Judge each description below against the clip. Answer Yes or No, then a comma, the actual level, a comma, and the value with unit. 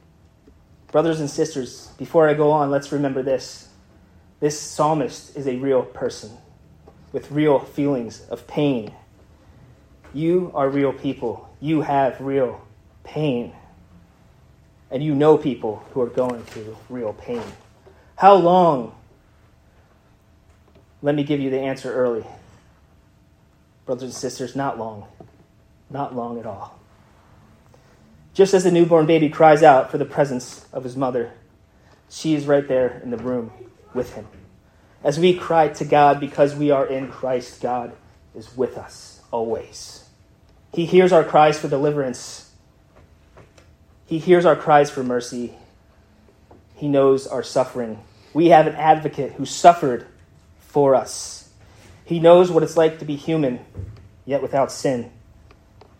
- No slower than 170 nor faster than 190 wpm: No, average, 140 wpm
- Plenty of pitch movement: Yes, wide, 5.8 semitones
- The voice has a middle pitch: No, low, 130 Hz